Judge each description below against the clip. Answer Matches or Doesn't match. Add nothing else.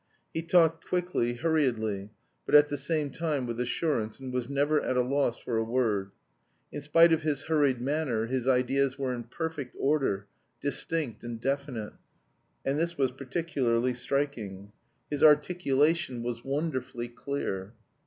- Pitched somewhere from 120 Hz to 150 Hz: Matches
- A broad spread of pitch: Doesn't match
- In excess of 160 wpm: Doesn't match